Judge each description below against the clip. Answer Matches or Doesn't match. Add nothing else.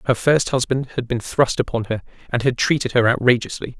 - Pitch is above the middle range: Doesn't match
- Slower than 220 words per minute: Matches